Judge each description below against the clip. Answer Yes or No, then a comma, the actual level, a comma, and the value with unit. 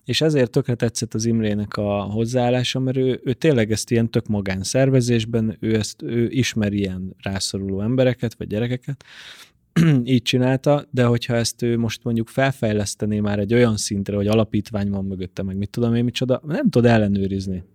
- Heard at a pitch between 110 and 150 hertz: Yes, low, 115 Hz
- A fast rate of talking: Yes, fast, 165 wpm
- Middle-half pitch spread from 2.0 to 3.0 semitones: No, average, 3.4 semitones